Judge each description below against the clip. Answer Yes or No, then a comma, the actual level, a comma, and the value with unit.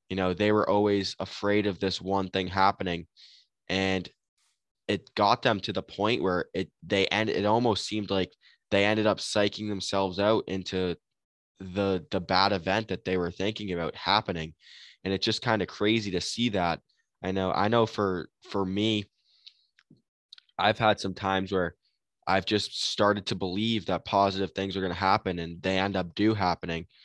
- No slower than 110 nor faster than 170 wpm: No, average, 180 wpm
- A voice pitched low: Yes, very low, 95 Hz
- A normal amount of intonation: No, narrow, 2.0 semitones